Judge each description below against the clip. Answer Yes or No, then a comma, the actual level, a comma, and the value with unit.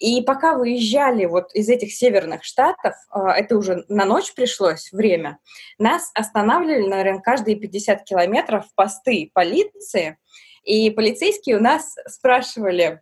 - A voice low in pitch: No, high, 215 Hz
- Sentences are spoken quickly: No, average, 125 wpm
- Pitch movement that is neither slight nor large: Yes, average, 4.5 semitones